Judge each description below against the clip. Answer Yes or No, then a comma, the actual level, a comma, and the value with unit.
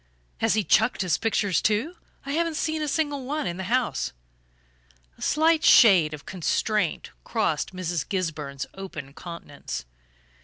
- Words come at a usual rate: Yes, average, 145 wpm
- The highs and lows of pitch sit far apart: Yes, wide, 8.8 semitones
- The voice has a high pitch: Yes, high, 195 Hz